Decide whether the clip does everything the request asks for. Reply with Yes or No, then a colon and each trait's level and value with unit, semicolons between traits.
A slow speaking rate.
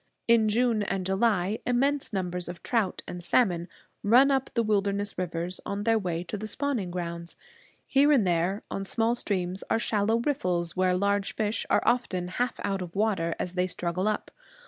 No: average, 180 wpm